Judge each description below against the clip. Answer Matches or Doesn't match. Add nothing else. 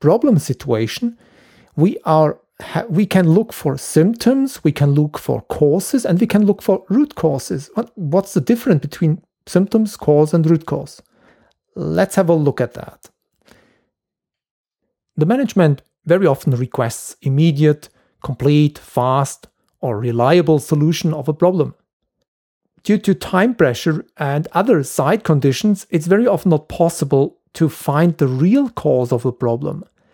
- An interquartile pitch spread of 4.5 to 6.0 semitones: Matches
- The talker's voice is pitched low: Doesn't match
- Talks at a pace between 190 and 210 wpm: Doesn't match